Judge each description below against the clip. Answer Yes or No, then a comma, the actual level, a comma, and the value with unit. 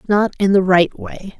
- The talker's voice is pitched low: No, high, 190 Hz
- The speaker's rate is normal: No, fast, 215 wpm